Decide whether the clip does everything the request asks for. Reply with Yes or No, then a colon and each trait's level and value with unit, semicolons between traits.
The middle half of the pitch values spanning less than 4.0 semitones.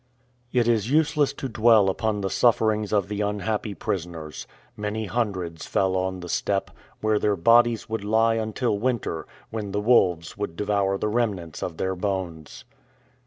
Yes: average, 3.0 semitones